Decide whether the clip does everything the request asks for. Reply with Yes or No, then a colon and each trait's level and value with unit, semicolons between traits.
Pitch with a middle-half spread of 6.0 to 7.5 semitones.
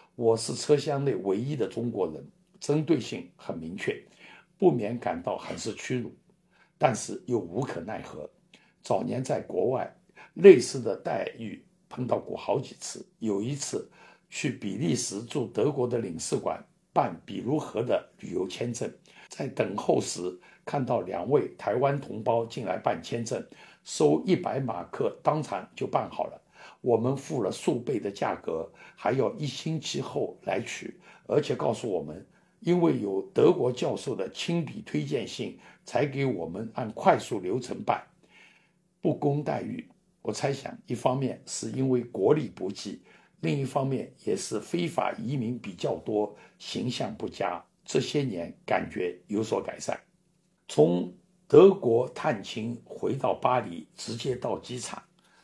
No: wide, 5.5 semitones